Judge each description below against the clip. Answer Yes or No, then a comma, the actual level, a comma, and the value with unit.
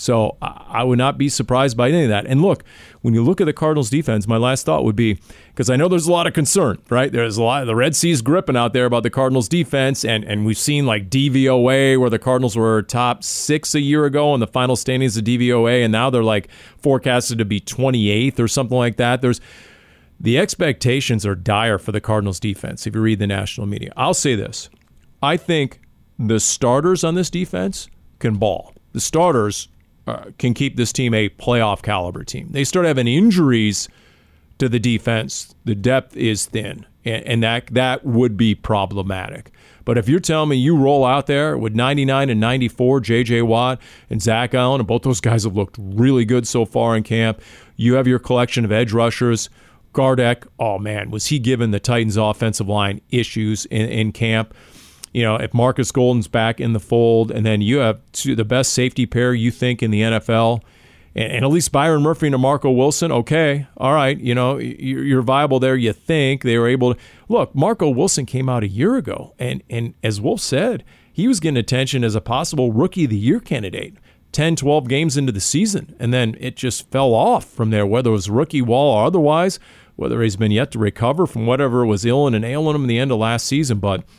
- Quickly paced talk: Yes, fast, 215 wpm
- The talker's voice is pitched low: Yes, low, 120 Hz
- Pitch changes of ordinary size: Yes, average, 3.4 semitones